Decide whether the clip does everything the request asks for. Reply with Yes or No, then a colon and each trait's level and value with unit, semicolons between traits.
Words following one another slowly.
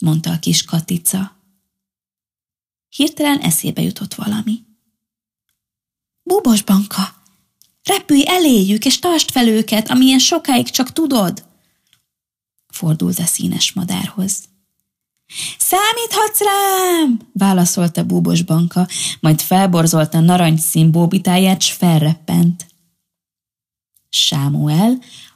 Yes: slow, 85 wpm